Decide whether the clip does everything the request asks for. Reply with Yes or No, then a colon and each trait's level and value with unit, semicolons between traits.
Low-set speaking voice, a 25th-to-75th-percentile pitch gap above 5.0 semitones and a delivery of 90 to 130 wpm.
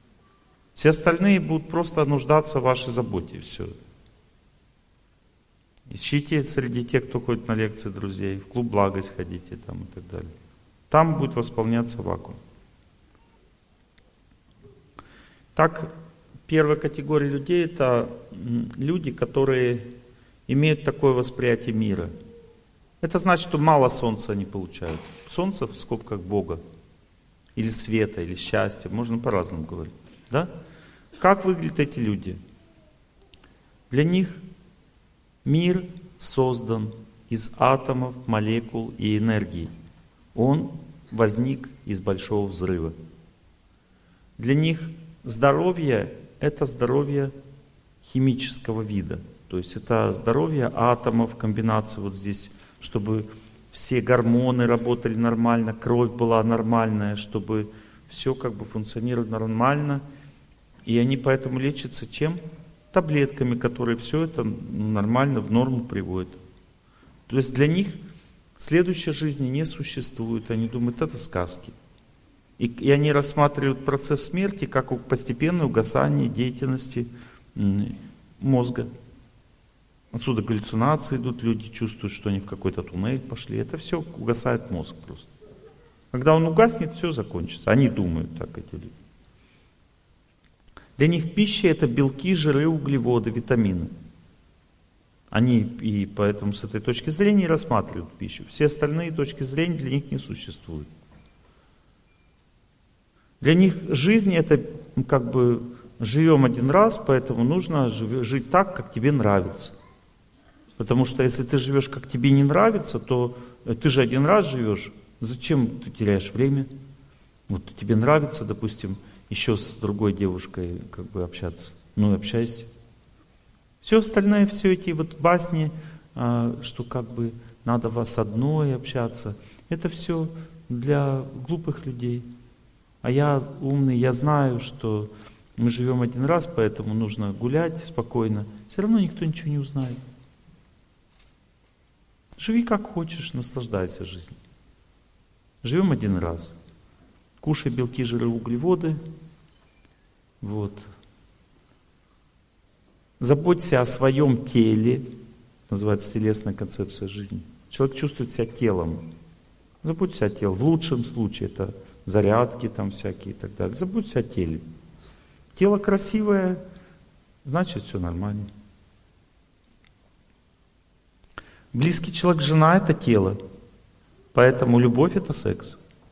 Yes: low, 120 Hz; wide, 5.6 semitones; average, 115 wpm